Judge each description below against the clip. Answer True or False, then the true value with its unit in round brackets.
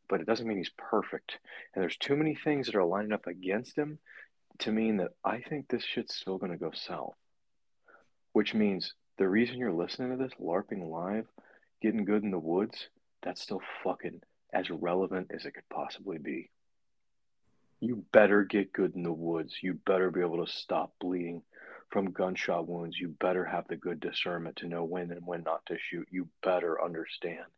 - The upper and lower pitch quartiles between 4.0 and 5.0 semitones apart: True (4.3 semitones)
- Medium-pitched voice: False (100 Hz)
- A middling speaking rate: True (190 wpm)